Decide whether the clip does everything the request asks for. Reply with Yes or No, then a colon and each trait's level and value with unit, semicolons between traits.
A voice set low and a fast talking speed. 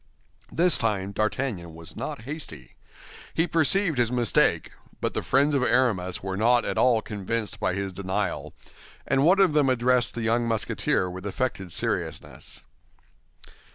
No: low, 115 Hz; average, 150 wpm